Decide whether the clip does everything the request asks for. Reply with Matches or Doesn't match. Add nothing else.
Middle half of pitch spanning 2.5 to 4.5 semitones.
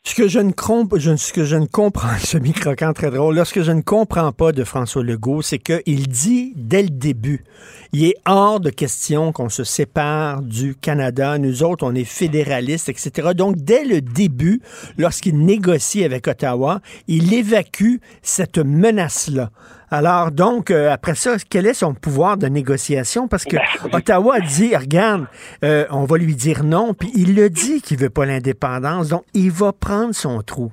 Doesn't match